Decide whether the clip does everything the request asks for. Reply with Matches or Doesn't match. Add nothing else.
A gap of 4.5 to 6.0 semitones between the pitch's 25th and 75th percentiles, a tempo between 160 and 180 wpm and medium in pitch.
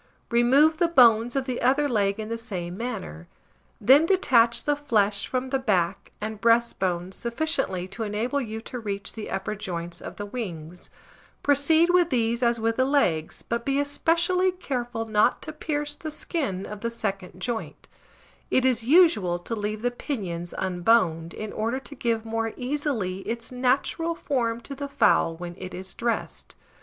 Doesn't match